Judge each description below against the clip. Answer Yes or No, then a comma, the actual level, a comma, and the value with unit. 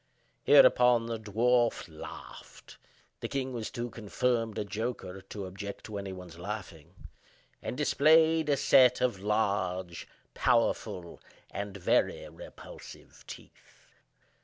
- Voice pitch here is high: No, low, 110 Hz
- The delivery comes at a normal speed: No, slow, 115 wpm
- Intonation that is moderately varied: Yes, average, 4.2 semitones